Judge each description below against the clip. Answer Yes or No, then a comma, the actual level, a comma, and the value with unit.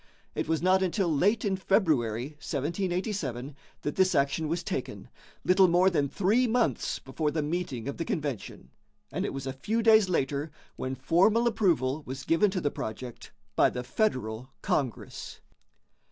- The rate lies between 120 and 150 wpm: No, average, 160 wpm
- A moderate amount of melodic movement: No, wide, 6.1 semitones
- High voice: No, medium, 160 Hz